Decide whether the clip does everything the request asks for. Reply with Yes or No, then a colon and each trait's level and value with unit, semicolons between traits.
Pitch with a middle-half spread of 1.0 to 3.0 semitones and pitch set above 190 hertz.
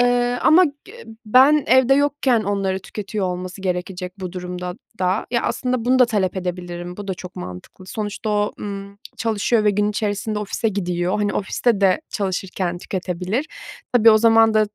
No: average, 3.7 semitones; high, 205 Hz